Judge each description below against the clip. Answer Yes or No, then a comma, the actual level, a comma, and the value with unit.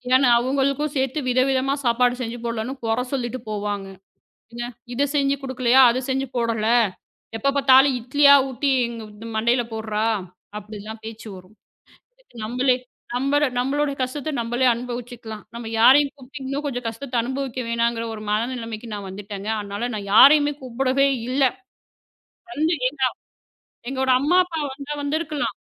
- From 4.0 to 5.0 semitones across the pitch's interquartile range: No, average, 3.3 semitones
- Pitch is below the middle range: No, very high, 250 Hz